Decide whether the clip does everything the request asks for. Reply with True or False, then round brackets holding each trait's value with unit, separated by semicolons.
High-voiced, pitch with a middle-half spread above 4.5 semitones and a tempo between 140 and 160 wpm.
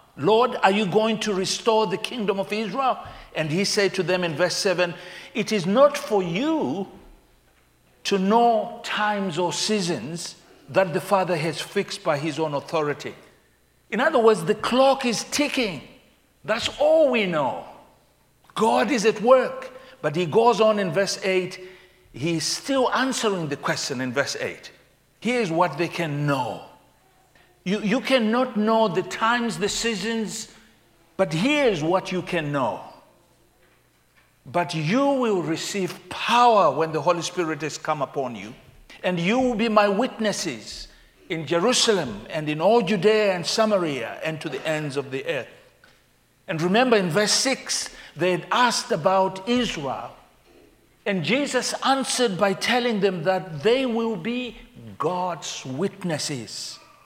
True (195 Hz; 5.3 semitones; 150 wpm)